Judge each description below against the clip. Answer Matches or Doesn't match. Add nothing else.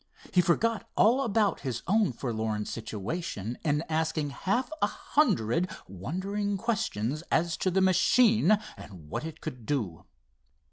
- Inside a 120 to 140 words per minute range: Matches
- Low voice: Doesn't match